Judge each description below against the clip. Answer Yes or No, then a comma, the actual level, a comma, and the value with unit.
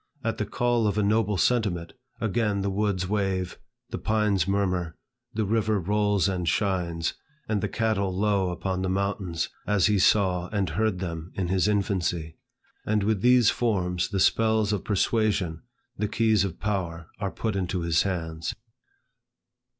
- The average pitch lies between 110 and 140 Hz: No, low, 100 Hz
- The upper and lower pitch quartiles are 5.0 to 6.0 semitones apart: No, average, 2.8 semitones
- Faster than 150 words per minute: Yes, average, 160 wpm